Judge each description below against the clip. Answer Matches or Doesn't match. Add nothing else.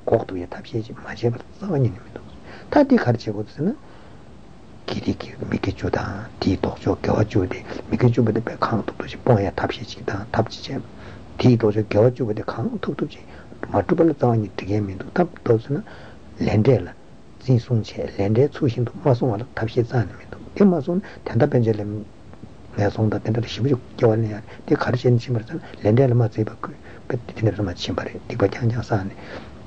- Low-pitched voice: Matches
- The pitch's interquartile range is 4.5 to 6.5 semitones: Doesn't match